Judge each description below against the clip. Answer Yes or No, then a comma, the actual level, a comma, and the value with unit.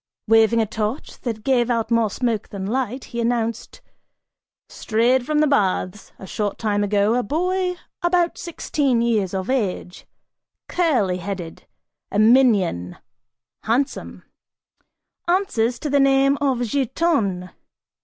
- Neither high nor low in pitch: No, high, 230 Hz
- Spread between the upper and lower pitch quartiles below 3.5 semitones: No, average, 4.7 semitones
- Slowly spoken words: Yes, slow, 125 wpm